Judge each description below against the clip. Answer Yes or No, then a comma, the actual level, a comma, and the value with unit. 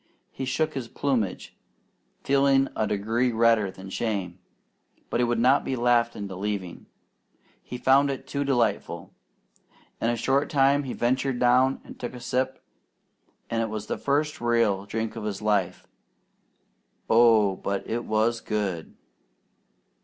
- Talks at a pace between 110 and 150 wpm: Yes, average, 145 wpm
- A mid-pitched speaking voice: No, low, 120 Hz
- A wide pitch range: No, average, 3.8 semitones